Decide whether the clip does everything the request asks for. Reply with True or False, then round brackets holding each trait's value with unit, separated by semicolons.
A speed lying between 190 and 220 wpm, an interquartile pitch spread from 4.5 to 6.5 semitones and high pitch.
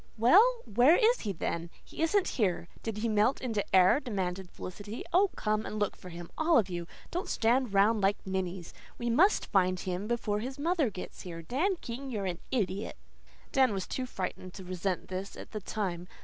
True (195 wpm; 5.6 semitones; 210 Hz)